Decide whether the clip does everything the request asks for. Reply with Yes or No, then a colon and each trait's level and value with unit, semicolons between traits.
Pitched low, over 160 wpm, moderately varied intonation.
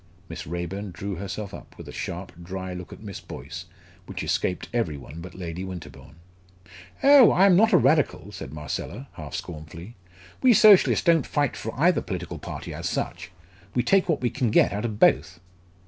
No: very low, 95 Hz; average, 185 wpm; wide, 7.9 semitones